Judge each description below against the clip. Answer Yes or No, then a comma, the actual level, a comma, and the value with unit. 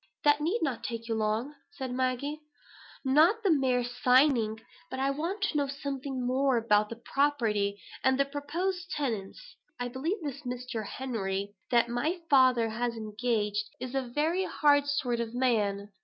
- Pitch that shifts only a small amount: No, average, 4.0 semitones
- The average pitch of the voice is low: No, very high, 255 Hz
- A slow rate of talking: No, average, 160 wpm